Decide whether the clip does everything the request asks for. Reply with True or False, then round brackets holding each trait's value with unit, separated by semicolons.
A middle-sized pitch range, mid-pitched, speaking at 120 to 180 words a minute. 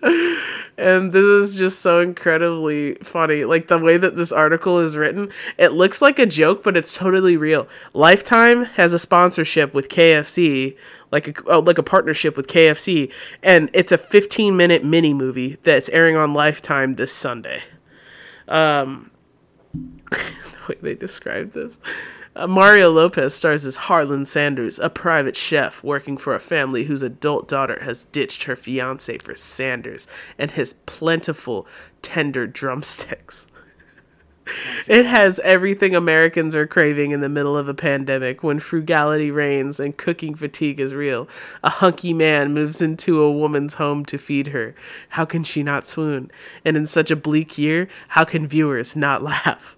True (3.1 semitones; 160 Hz; 160 wpm)